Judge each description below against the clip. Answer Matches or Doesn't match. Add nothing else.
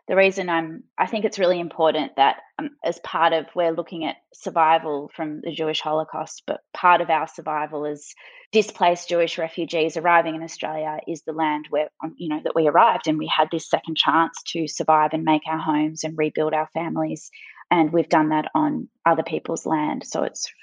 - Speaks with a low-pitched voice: Doesn't match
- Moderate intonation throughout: Doesn't match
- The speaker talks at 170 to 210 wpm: Matches